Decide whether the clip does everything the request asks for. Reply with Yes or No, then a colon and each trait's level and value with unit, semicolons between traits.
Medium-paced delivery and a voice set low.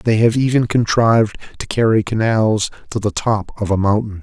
Yes: average, 185 wpm; low, 110 Hz